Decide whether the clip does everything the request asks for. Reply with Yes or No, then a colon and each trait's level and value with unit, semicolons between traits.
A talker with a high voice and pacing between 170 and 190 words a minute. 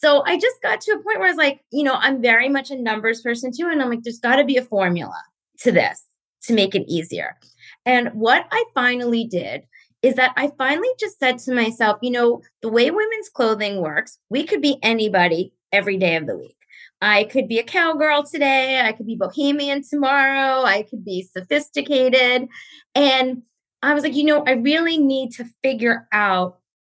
No: very high, 255 Hz; fast, 205 wpm